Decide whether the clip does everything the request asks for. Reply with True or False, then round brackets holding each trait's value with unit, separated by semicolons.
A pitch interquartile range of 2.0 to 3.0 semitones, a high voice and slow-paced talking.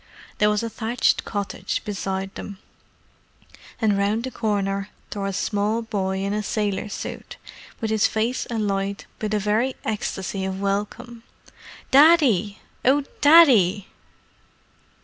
True (2.6 semitones; 210 Hz; 130 wpm)